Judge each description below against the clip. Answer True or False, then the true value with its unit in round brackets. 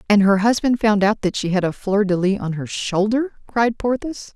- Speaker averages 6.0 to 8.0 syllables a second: False (4.9 syllables/s)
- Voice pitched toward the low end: False (210 Hz)